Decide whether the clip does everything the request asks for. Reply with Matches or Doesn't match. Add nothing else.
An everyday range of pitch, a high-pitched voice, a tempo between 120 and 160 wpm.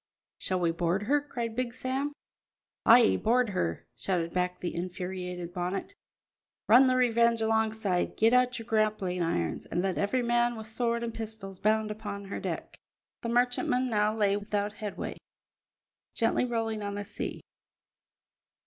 Matches